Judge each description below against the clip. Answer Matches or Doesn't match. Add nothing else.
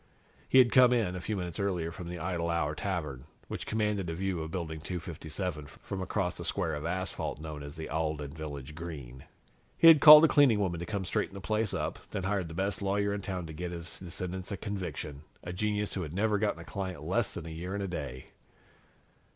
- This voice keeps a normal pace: Doesn't match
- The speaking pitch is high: Doesn't match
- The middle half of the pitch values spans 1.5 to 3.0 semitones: Doesn't match